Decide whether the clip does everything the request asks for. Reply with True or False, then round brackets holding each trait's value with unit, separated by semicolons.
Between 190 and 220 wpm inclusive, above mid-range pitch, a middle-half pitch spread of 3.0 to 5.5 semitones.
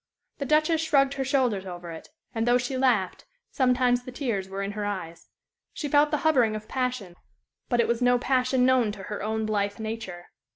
True (200 wpm; 245 Hz; 4.2 semitones)